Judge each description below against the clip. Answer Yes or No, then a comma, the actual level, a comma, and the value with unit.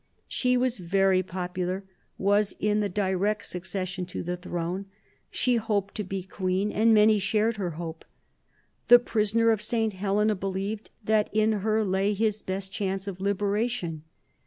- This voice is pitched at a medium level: No, high, 200 Hz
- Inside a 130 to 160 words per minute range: Yes, average, 155 wpm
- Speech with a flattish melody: Yes, narrow, 2.3 semitones